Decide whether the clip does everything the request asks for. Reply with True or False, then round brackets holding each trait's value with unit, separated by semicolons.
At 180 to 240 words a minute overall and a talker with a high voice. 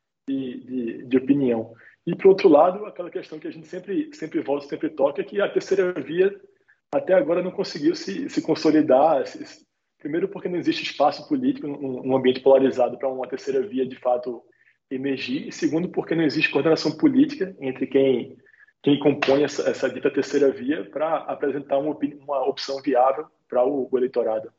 False (185 wpm; 155 Hz)